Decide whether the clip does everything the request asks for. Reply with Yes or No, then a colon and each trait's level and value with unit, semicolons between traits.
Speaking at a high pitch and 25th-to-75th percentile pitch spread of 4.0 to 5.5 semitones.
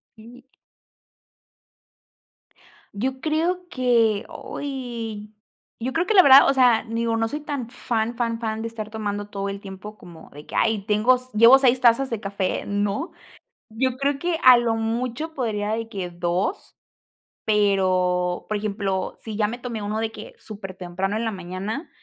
No: high, 225 Hz; average, 3.6 semitones